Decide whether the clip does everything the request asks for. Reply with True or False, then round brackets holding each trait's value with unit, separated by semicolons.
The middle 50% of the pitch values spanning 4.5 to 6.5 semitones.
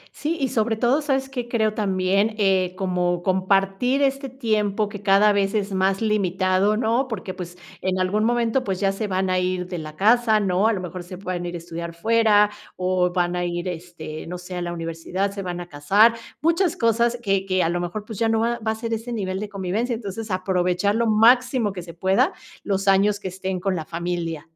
False (3.6 semitones)